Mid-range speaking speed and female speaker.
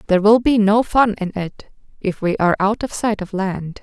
No: fast, 220 wpm; female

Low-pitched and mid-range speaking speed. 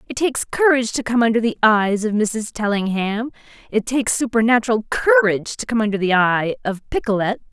No: high, 225 Hz; average, 175 wpm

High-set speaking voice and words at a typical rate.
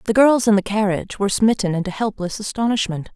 Yes: high, 205 Hz; average, 190 wpm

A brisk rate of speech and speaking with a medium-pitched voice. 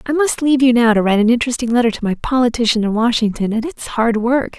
No: fast, 250 wpm; high, 240 Hz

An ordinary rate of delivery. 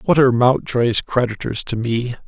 Yes: average, 160 wpm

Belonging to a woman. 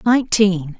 Yes: female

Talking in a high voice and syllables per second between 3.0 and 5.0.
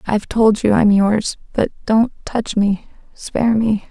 Yes: high, 215 Hz; 4.2 syllables/s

